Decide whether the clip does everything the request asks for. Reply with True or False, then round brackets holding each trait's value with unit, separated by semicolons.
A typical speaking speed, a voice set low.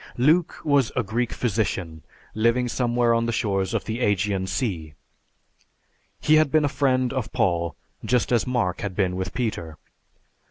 True (160 wpm; 115 Hz)